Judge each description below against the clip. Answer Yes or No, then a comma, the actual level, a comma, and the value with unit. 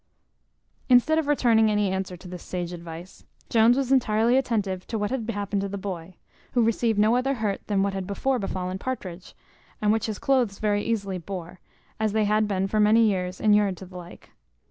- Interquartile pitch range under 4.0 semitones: Yes, average, 3.3 semitones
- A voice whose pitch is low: No, high, 205 Hz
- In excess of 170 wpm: Yes, average, 200 wpm